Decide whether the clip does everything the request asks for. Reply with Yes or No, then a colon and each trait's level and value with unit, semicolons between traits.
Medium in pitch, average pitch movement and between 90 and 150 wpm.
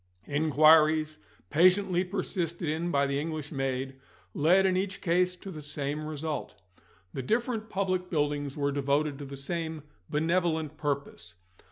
Yes: medium, 155 Hz; average, 3.9 semitones; average, 140 wpm